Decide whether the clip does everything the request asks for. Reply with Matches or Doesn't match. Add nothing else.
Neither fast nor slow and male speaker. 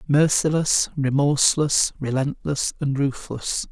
Doesn't match